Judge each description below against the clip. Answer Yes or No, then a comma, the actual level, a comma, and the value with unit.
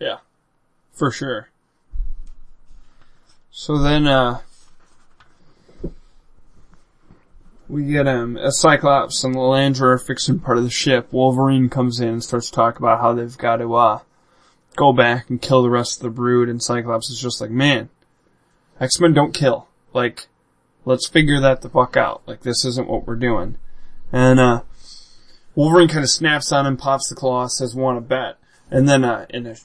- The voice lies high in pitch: No, low, 130 Hz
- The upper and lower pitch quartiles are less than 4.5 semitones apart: Yes, narrow, 2.4 semitones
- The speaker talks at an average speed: Yes, average, 170 wpm